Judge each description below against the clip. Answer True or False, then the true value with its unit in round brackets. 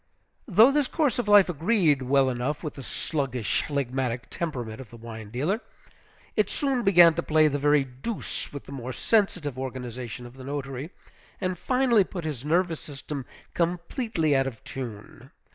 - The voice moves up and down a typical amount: False (6.0 semitones)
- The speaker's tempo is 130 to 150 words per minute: False (165 wpm)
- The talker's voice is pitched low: False (145 Hz)